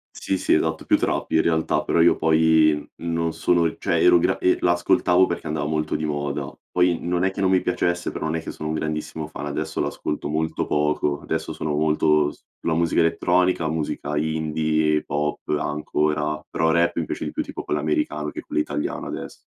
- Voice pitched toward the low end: Yes, very low, 80 Hz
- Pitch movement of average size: No, narrow, 1.8 semitones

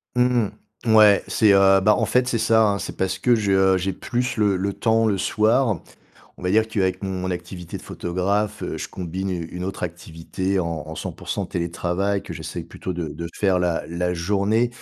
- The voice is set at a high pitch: No, very low, 95 Hz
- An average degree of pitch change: Yes, average, 3.1 semitones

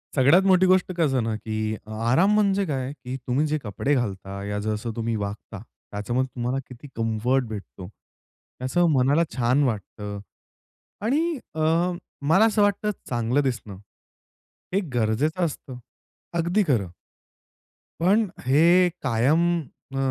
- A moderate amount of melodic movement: No, wide, 7.5 semitones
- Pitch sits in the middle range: No, low, 130 Hz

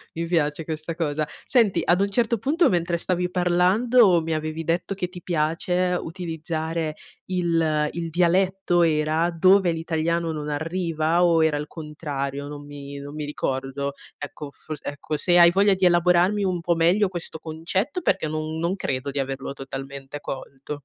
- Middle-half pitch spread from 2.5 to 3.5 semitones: Yes, average, 2.9 semitones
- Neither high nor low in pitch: Yes, medium, 165 Hz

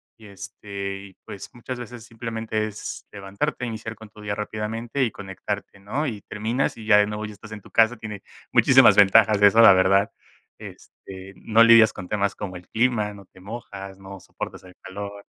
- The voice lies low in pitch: Yes, low, 105 Hz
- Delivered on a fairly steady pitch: Yes, narrow, 2.3 semitones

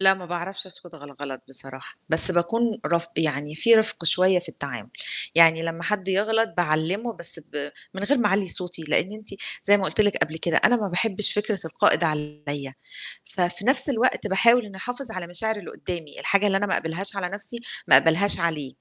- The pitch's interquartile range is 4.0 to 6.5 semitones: Yes, average, 4.3 semitones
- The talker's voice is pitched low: No, medium, 185 Hz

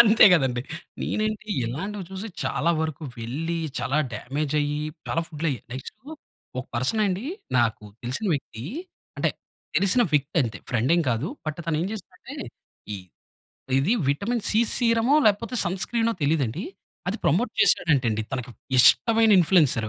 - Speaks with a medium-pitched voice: Yes, medium, 160 Hz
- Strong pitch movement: Yes, wide, 8.1 semitones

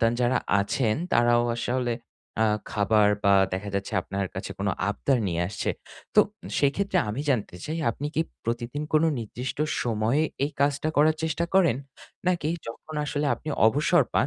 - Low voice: Yes, low, 120 Hz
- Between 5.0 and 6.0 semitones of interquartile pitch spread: Yes, wide, 5.5 semitones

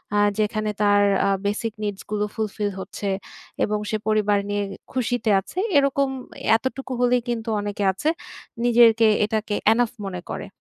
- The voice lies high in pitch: Yes, high, 215 Hz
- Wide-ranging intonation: No, average, 2.7 semitones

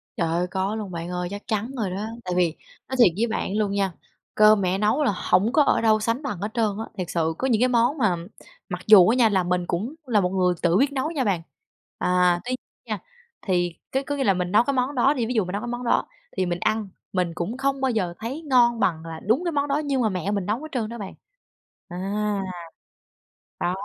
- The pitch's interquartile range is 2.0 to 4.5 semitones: No, average, 5.3 semitones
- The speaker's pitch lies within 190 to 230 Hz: Yes, high, 210 Hz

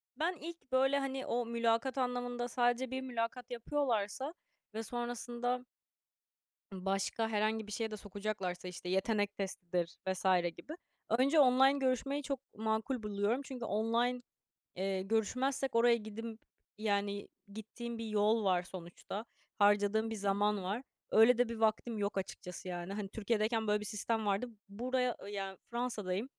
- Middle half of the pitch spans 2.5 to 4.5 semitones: Yes, average, 3.4 semitones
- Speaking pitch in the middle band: No, high, 225 Hz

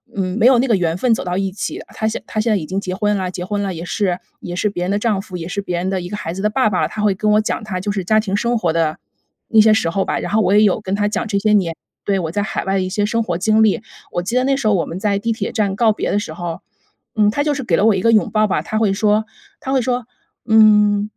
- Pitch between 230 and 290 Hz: No, high, 205 Hz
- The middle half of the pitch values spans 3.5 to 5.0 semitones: No, average, 2.8 semitones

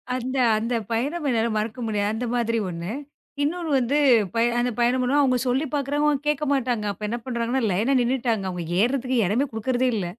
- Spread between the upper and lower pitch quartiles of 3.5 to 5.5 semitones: No, average, 3.1 semitones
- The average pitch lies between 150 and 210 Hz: No, high, 245 Hz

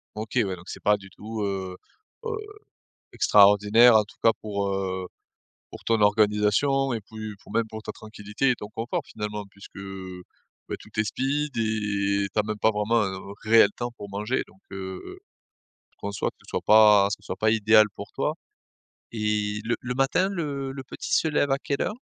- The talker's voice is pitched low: Yes, low, 105 Hz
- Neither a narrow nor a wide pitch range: No, narrow, 2.3 semitones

